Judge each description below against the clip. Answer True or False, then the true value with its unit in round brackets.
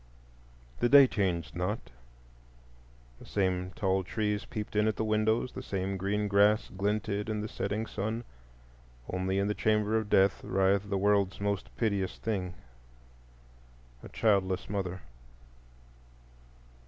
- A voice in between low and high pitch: False (100 Hz)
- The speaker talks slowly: True (130 wpm)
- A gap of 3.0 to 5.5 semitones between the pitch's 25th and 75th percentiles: False (2.4 semitones)